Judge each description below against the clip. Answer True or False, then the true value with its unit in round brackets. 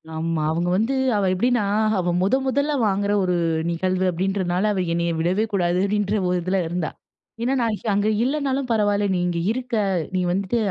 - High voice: True (195 Hz)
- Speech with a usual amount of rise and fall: True (4.1 semitones)